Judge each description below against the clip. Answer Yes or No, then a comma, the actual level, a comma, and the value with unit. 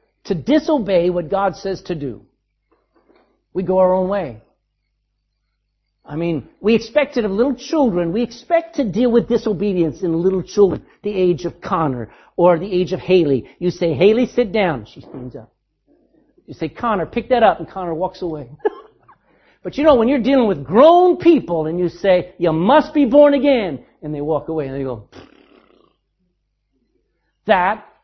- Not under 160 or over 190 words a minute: Yes, average, 175 wpm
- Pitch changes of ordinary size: No, wide, 6.8 semitones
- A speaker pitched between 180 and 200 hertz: Yes, medium, 185 Hz